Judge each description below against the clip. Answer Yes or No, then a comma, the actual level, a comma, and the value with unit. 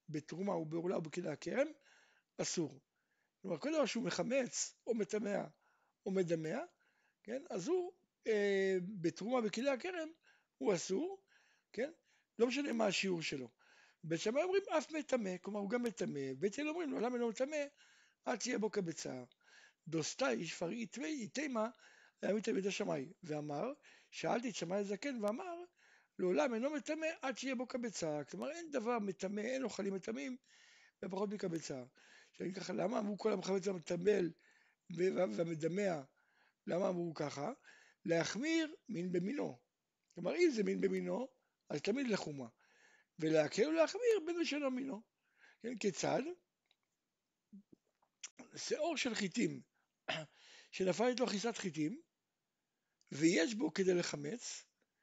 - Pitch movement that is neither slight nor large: No, wide, 7.3 semitones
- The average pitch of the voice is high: Yes, high, 215 Hz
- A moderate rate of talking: Yes, average, 130 wpm